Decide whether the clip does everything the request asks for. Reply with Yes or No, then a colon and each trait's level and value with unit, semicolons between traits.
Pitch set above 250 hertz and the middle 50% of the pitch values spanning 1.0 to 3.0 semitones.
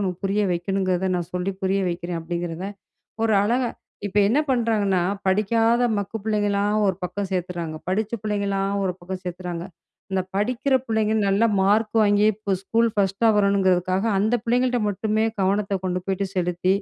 No: high, 200 Hz; average, 2.7 semitones